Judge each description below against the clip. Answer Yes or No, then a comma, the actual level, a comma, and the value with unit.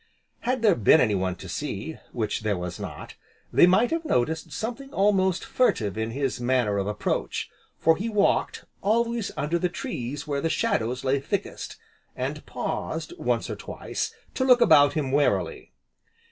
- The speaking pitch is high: No, medium, 150 Hz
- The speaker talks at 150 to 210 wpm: Yes, average, 160 wpm